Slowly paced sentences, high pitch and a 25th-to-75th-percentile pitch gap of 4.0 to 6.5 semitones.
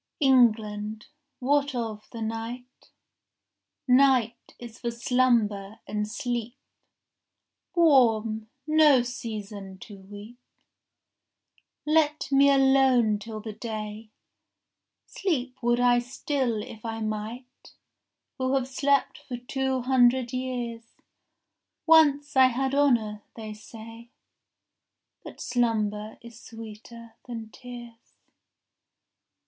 No: slow, 100 wpm; high, 240 Hz; average, 3.1 semitones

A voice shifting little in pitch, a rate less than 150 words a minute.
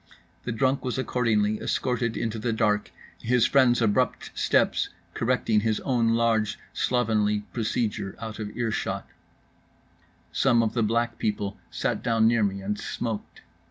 Yes: narrow, 2.1 semitones; average, 140 wpm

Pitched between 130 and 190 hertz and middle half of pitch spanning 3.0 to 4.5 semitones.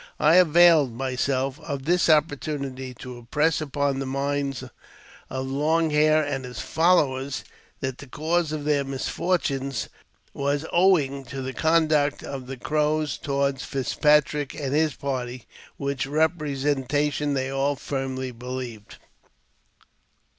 No: medium, 140 Hz; narrow, 2.4 semitones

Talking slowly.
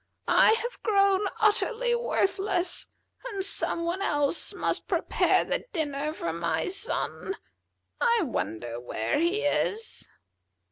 Yes: slow, 120 wpm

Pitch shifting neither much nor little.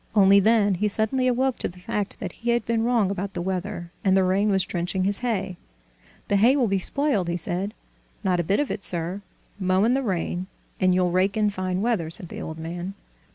Yes: average, 3.2 semitones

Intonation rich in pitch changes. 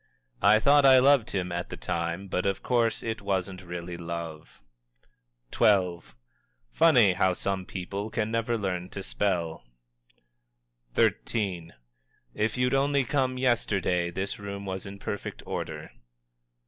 No: average, 4.2 semitones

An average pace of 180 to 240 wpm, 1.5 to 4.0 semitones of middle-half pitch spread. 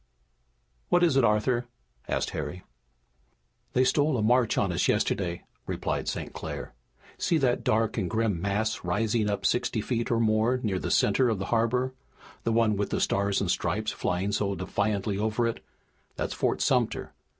No: average, 170 wpm; average, 3.1 semitones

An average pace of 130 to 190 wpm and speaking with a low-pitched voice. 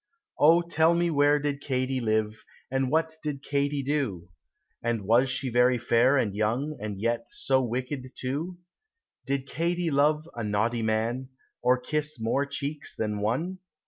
Yes: average, 155 wpm; low, 130 Hz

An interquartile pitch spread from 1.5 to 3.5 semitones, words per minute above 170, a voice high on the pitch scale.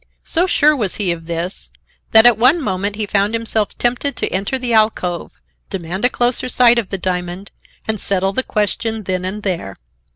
No: average, 4.4 semitones; average, 190 wpm; high, 210 Hz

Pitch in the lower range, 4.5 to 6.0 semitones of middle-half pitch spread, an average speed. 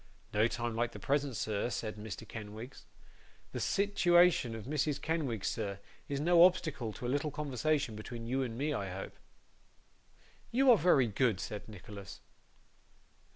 Yes: low, 125 Hz; wide, 5.6 semitones; average, 155 wpm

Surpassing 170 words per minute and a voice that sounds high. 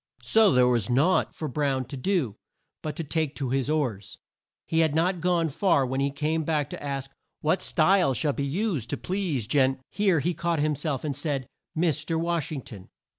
No: fast, 205 wpm; medium, 150 Hz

